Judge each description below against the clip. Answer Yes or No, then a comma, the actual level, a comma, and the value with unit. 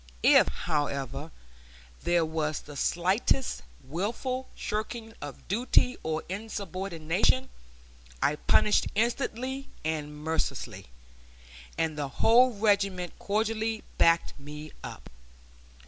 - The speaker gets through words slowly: Yes, slow, 95 wpm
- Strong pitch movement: Yes, wide, 6.3 semitones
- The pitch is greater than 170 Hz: Yes, medium, 185 Hz